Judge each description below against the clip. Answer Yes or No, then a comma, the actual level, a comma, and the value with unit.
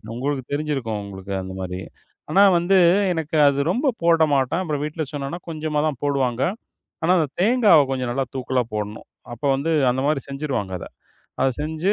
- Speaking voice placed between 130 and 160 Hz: Yes, medium, 140 Hz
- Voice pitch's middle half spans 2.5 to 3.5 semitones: No, average, 4.2 semitones